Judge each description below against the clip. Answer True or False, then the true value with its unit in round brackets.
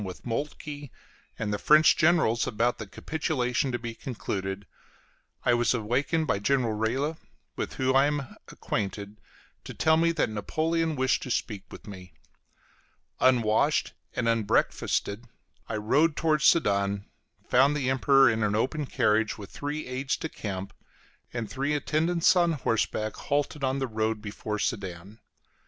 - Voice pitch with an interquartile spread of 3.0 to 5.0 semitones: False (5.5 semitones)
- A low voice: True (125 Hz)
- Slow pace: False (150 wpm)